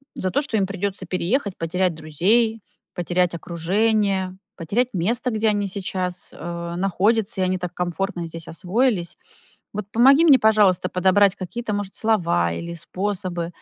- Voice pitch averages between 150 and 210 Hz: Yes, high, 190 Hz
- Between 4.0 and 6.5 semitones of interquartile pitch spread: No, average, 3.6 semitones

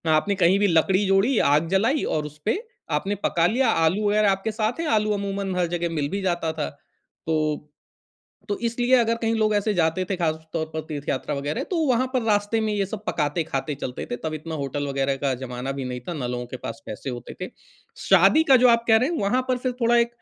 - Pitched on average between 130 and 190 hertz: Yes, medium, 185 Hz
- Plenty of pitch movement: Yes, wide, 6.2 semitones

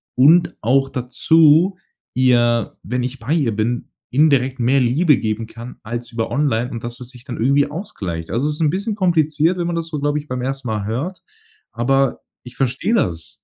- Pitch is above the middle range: No, low, 130 Hz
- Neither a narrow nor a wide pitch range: Yes, average, 4.3 semitones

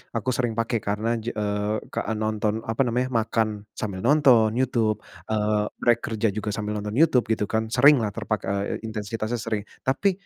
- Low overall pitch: Yes, low, 110 Hz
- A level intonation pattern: Yes, narrow, 2.1 semitones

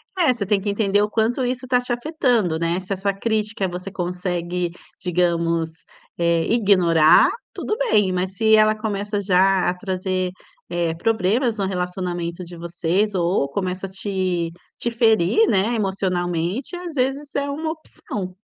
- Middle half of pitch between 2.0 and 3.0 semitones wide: No, average, 3.9 semitones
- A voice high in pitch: Yes, high, 195 Hz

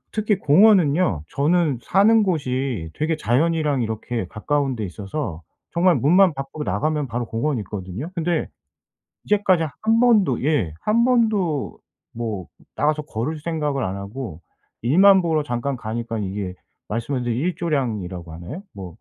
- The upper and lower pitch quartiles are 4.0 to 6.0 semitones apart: No, wide, 7.2 semitones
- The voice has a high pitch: No, medium, 140 Hz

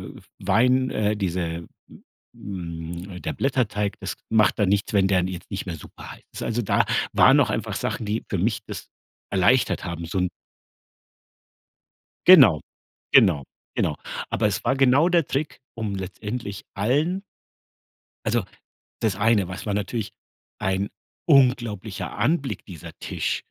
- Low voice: Yes, low, 105 Hz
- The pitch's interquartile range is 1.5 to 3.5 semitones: No, average, 4.9 semitones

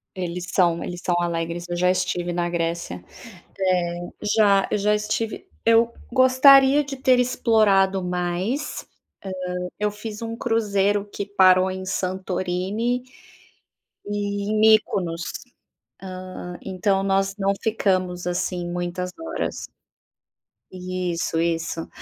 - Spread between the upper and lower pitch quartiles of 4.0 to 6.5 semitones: No, average, 3.2 semitones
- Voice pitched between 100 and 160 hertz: No, high, 190 Hz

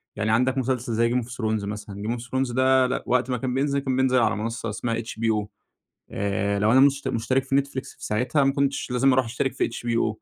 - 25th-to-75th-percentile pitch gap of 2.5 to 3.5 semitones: Yes, average, 2.8 semitones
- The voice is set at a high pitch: No, low, 125 Hz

